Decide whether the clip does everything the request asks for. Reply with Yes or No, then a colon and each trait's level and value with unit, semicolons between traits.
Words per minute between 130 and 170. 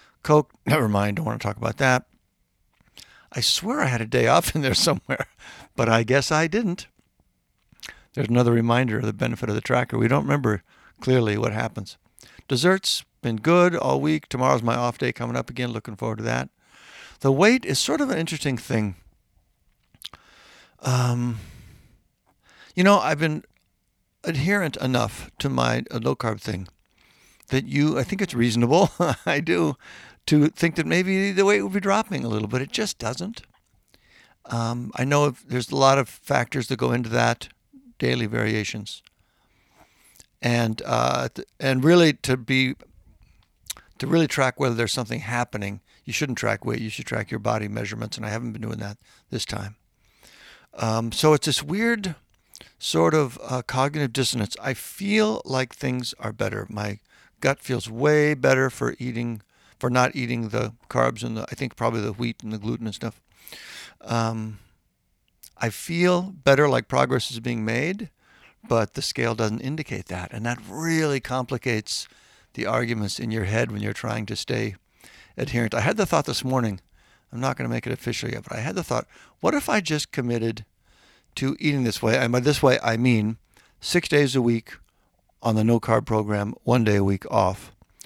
No: average, 180 wpm